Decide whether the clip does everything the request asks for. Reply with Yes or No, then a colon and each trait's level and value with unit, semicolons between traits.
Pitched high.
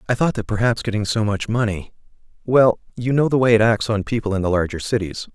No: low, 110 Hz